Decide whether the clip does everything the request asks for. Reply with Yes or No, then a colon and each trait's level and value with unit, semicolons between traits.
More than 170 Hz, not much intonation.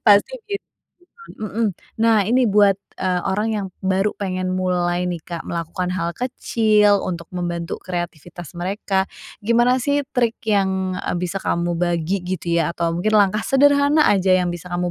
No: high, 190 Hz; average, 3.5 semitones